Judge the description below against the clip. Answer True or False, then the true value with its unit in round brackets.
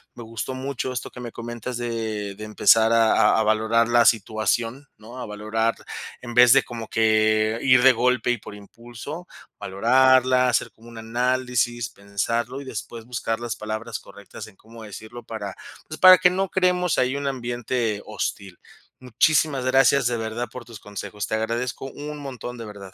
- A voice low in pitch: True (115 Hz)